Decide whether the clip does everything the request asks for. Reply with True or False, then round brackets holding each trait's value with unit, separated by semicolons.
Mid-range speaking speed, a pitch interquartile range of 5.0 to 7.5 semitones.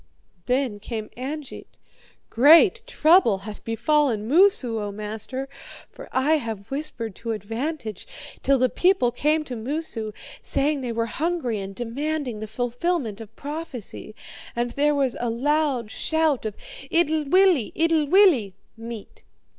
False (130 wpm; 5.5 semitones)